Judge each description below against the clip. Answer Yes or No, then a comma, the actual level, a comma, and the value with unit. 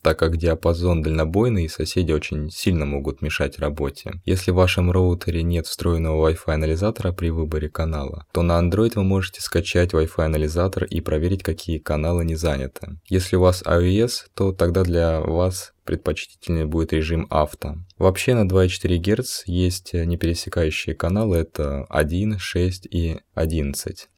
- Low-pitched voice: Yes, very low, 85 Hz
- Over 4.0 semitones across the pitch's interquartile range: No, average, 2.7 semitones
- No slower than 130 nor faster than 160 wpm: Yes, average, 150 wpm